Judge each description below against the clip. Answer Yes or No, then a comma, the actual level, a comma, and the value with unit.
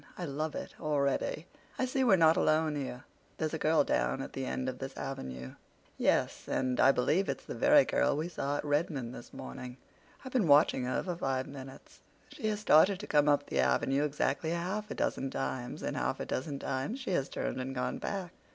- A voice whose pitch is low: No, medium, 145 Hz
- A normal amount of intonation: Yes, average, 4.6 semitones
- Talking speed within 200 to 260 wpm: Yes, fast, 205 wpm